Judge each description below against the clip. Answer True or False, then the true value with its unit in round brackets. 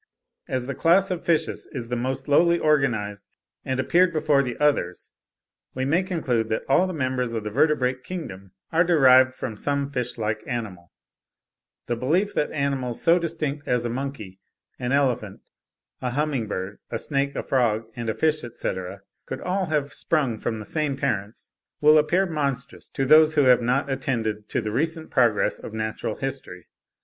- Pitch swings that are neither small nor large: True (4.8 semitones)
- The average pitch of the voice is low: True (130 Hz)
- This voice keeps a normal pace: True (175 wpm)